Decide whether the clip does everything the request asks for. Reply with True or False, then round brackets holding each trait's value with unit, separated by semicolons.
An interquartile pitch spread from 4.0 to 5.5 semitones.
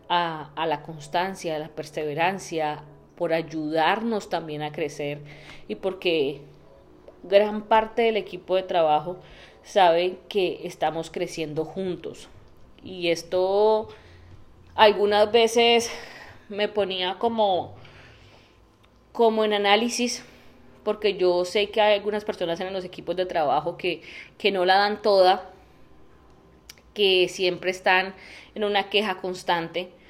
True (4.6 semitones)